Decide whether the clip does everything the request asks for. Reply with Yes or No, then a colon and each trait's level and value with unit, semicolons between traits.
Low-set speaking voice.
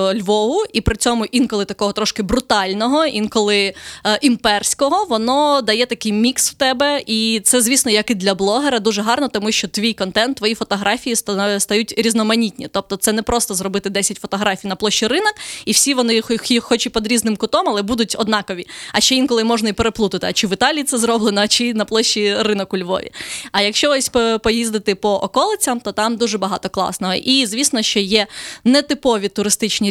No: high, 220 Hz